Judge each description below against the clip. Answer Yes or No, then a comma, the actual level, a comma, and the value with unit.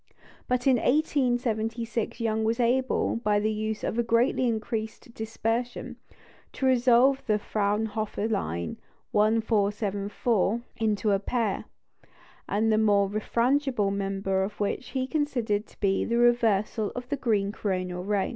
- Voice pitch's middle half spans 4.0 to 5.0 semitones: No, average, 2.7 semitones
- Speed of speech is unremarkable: No, slow, 125 wpm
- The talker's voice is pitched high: Yes, high, 220 Hz